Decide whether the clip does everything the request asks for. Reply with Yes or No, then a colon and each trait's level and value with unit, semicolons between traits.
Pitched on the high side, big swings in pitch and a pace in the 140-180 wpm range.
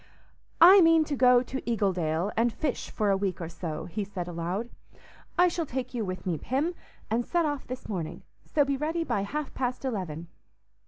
No: high, 235 Hz; wide, 7.6 semitones; average, 195 wpm